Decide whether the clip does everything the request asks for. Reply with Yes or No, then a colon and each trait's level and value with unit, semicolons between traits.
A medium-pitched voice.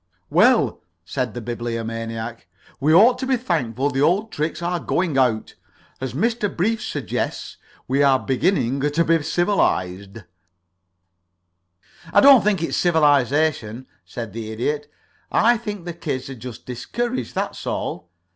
Yes: medium, 145 Hz